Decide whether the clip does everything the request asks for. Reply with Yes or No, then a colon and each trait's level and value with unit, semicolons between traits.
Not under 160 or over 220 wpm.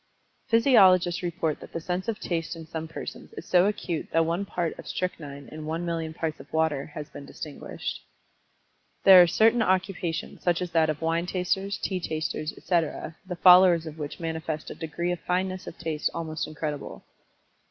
Yes: average, 180 wpm